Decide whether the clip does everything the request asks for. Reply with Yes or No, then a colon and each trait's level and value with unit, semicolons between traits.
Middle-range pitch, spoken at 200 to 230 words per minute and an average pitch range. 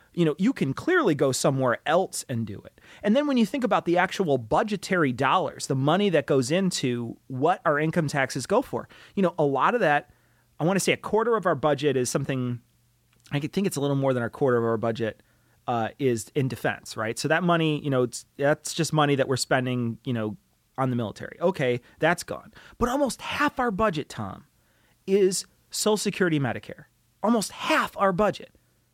No: medium, 145 Hz; fast, 205 wpm; wide, 7.0 semitones